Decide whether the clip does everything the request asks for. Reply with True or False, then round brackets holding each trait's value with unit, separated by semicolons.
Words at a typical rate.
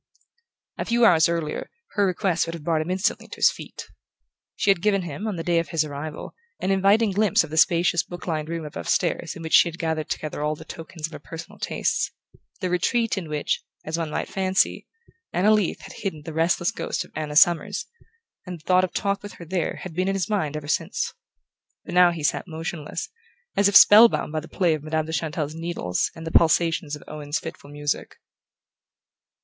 False (215 wpm)